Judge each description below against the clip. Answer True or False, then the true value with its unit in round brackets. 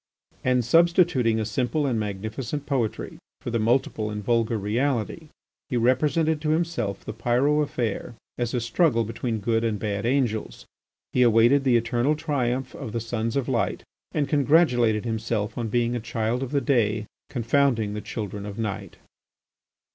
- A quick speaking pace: False (160 wpm)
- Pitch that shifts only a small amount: False (3.7 semitones)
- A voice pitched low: True (120 Hz)